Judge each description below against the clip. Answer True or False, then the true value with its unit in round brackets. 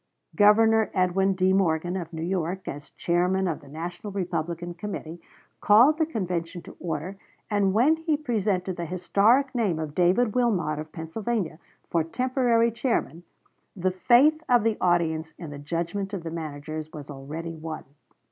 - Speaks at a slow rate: False (155 wpm)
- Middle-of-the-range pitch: True (180 Hz)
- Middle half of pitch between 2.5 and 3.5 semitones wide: False (4.8 semitones)